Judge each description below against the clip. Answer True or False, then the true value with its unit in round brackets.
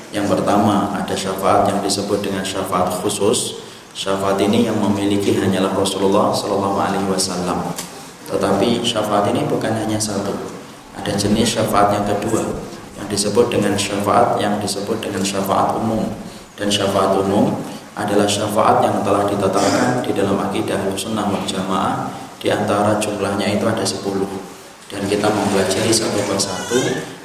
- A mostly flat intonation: True (1.1 semitones)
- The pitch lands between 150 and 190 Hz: False (100 Hz)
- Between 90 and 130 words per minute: False (140 wpm)